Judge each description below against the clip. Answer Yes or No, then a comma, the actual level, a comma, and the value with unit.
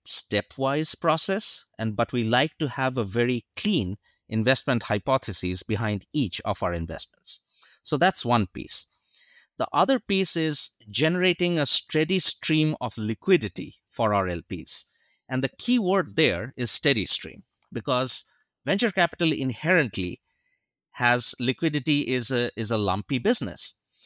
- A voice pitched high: No, low, 130 Hz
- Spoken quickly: No, slow, 135 wpm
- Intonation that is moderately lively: No, wide, 6.2 semitones